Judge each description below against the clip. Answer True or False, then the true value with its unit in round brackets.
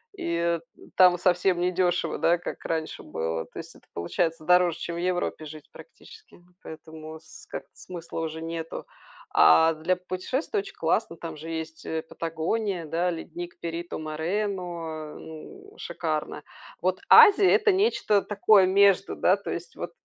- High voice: False (175 Hz)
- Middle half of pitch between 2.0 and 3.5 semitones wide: True (2.9 semitones)